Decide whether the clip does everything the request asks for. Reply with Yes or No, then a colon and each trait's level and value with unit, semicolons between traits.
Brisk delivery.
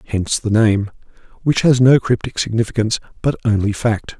No: average, 155 wpm